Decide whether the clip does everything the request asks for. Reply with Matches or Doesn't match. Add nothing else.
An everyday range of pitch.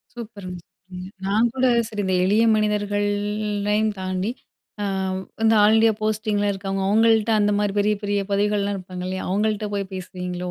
Doesn't match